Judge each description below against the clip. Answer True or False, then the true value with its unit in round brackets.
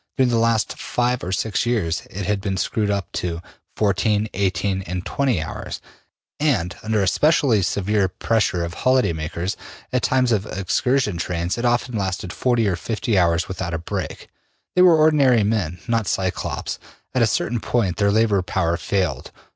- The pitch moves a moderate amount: True (4.6 semitones)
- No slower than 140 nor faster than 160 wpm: False (170 wpm)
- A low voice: True (100 Hz)